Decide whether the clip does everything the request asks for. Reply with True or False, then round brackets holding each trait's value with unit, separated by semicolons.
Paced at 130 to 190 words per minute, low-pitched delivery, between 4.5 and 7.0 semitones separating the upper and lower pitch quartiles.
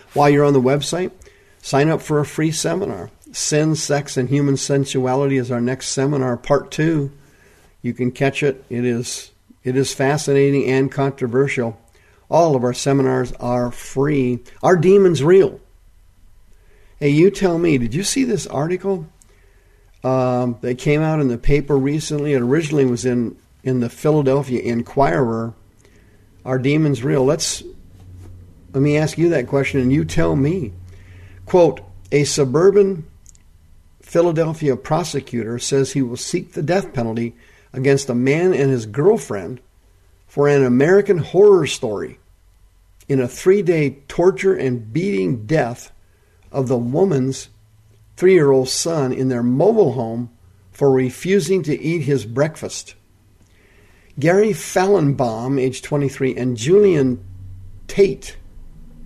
True (140 wpm; 130 Hz; 5.3 semitones)